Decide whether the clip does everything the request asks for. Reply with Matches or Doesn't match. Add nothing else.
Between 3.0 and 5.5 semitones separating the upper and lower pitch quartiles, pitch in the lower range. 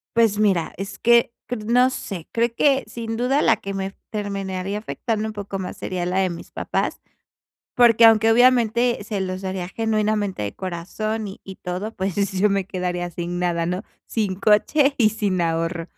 Doesn't match